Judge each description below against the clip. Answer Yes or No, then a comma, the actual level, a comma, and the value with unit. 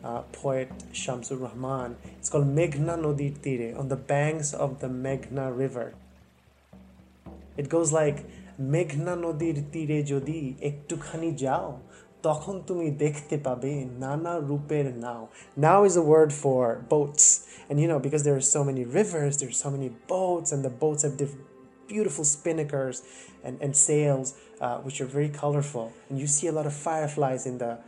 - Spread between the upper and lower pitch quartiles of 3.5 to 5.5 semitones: No, average, 2.8 semitones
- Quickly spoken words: No, average, 160 wpm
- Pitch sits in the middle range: Yes, medium, 145 Hz